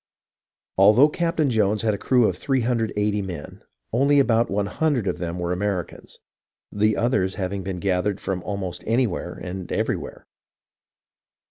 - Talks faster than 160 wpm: No, slow, 135 wpm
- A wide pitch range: No, average, 4.2 semitones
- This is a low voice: Yes, low, 105 Hz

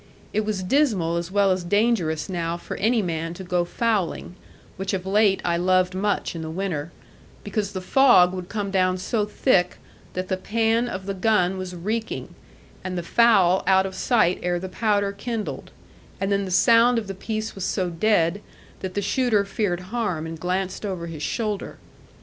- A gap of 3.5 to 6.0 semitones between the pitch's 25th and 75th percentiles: No, average, 3.0 semitones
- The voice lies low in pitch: No, high, 190 Hz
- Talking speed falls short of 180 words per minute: No, average, 185 wpm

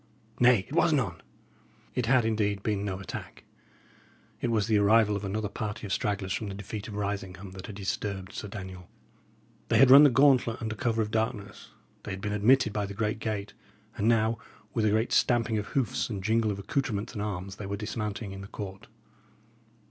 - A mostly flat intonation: Yes, narrow, 2.3 semitones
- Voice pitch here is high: No, low, 105 Hz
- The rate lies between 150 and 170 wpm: No, average, 200 wpm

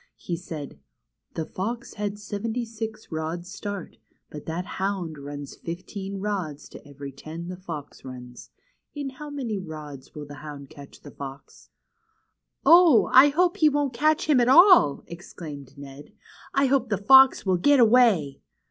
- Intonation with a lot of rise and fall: Yes, wide, 8.5 semitones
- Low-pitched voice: No, medium, 185 Hz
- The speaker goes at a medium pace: Yes, average, 155 wpm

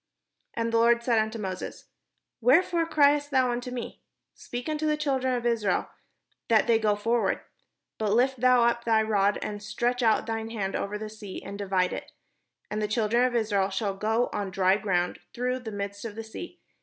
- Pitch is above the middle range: Yes, high, 225 Hz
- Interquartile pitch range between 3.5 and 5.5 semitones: No, average, 3.1 semitones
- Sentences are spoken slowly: No, average, 195 wpm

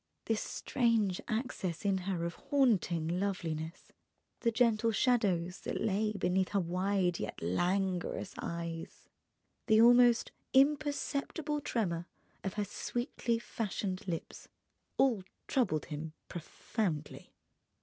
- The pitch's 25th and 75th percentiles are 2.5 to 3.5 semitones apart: No, average, 5.1 semitones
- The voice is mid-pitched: No, high, 195 Hz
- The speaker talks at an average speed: No, slow, 105 wpm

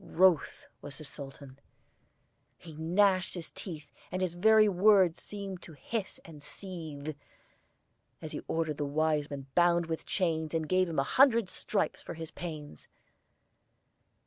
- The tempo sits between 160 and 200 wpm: No, average, 145 wpm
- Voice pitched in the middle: Yes, medium, 165 Hz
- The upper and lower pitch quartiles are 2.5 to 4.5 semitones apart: Yes, average, 3.6 semitones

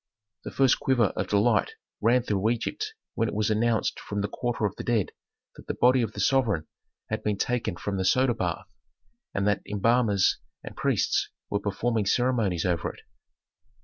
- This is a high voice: No, low, 110 Hz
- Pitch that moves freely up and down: No, average, 3.2 semitones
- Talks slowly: No, average, 180 wpm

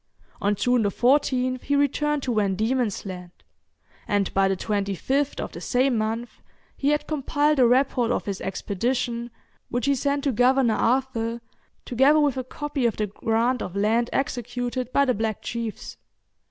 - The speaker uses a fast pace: No, average, 165 wpm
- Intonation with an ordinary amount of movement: Yes, average, 3.7 semitones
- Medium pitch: No, high, 245 Hz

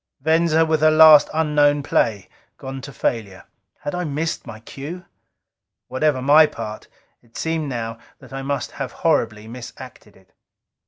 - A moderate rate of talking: Yes, average, 150 wpm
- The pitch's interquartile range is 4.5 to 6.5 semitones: Yes, average, 5.1 semitones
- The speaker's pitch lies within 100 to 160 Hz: Yes, medium, 140 Hz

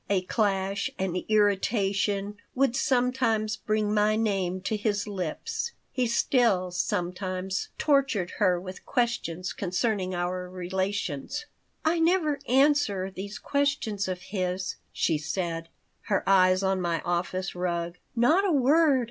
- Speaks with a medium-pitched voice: No, high, 200 Hz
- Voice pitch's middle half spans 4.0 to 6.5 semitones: Yes, average, 4.6 semitones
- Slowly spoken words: Yes, slow, 125 wpm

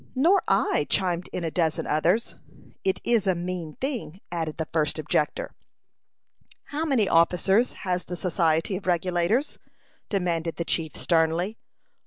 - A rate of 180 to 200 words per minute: No, average, 140 wpm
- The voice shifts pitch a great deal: No, average, 3.4 semitones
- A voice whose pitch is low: No, medium, 180 Hz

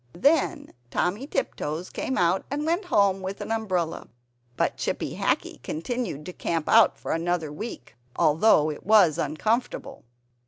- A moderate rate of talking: Yes, average, 145 wpm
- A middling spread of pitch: No, wide, 6.1 semitones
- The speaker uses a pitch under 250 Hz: Yes, high, 190 Hz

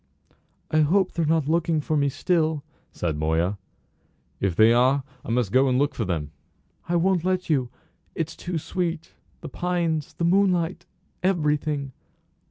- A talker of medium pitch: Yes, medium, 155 Hz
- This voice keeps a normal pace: Yes, average, 155 wpm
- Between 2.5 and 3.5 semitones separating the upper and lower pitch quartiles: No, average, 5.0 semitones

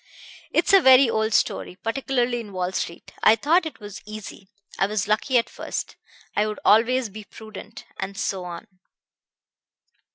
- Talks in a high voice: Yes, high, 215 Hz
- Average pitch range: Yes, average, 3.6 semitones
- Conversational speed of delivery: Yes, average, 160 wpm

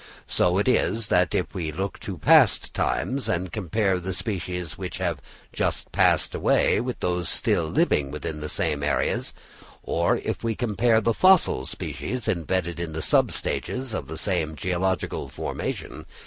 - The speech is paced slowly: No, average, 160 wpm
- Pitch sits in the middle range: No, very low, 90 Hz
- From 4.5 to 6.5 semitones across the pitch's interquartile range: Yes, average, 5.2 semitones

